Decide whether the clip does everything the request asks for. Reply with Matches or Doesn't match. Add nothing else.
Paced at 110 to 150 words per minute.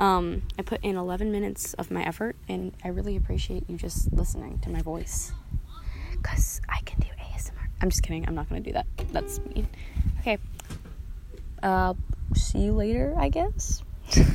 Doesn't match